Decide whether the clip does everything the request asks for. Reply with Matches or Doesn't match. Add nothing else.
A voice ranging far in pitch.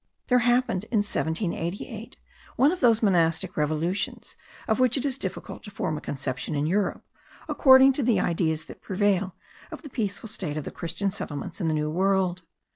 Matches